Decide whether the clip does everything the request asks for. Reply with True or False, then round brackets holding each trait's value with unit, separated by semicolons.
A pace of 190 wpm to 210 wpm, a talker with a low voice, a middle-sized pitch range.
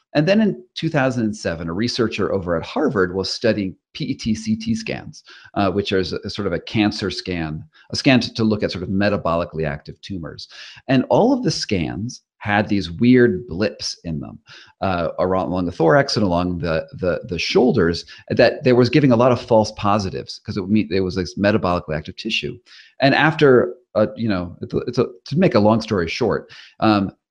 True (200 wpm; 105 Hz; 4.2 semitones)